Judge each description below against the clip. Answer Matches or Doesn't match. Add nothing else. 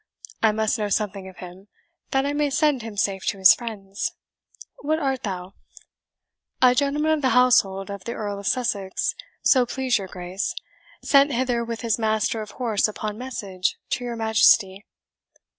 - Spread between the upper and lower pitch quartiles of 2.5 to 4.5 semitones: Matches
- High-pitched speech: Matches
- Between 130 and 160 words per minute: Doesn't match